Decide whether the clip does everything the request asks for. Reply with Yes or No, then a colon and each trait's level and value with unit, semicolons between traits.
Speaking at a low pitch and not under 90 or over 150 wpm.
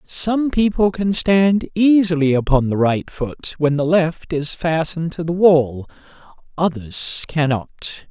No: medium, 165 Hz; average, 140 wpm